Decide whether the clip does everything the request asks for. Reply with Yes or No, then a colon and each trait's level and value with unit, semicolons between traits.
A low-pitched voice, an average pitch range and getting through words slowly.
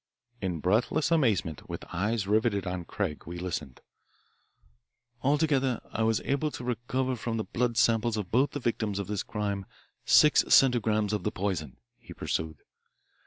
No: low, 110 Hz; average, 4.4 semitones; average, 160 wpm